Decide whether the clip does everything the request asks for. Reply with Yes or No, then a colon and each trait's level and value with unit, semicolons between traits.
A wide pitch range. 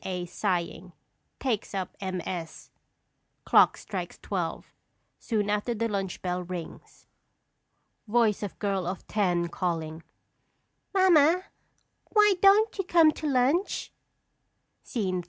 Yes: wide, 7.8 semitones